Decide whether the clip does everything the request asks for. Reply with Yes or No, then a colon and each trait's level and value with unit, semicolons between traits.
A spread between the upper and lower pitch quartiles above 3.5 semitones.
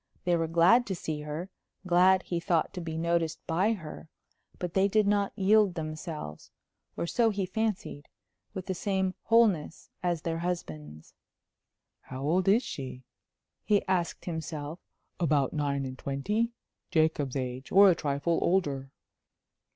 Yes: average, 4.2 semitones